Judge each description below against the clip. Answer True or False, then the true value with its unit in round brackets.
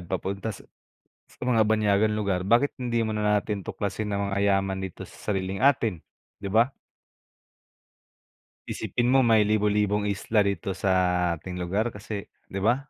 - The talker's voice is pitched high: False (105 Hz)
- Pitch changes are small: True (2.1 semitones)